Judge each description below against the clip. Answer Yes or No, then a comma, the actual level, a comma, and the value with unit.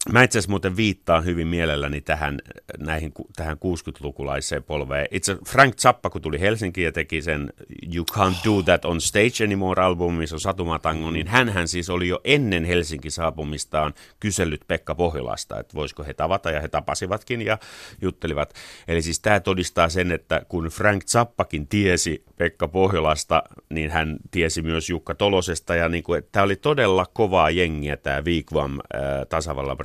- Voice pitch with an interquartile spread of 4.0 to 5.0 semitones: No, average, 3.5 semitones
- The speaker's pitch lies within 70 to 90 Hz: Yes, very low, 85 Hz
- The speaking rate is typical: No, fast, 165 wpm